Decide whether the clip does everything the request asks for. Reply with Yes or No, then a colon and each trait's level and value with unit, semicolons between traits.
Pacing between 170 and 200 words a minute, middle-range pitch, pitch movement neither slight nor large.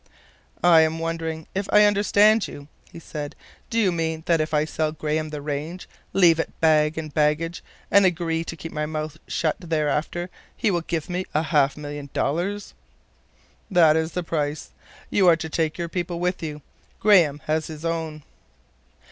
No: average, 175 wpm; medium, 160 Hz; narrow, 2.3 semitones